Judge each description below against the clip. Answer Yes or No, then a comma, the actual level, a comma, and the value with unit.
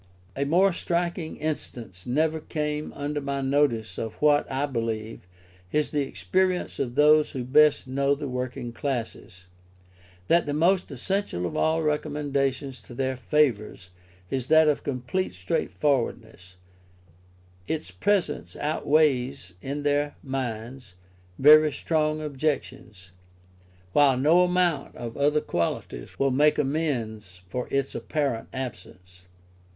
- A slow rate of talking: Yes, slow, 125 wpm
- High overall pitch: No, medium, 140 Hz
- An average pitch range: Yes, average, 3.9 semitones